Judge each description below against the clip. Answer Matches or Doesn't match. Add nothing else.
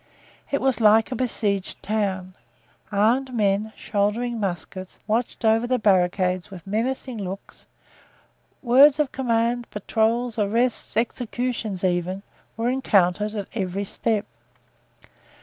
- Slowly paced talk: Matches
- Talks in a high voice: Matches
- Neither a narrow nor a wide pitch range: Matches